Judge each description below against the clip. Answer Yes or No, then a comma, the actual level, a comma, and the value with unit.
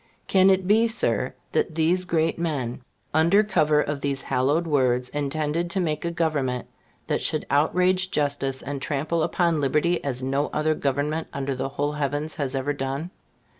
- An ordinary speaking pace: Yes, average, 170 wpm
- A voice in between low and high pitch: Yes, medium, 150 Hz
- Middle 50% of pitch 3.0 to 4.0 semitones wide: Yes, average, 3.4 semitones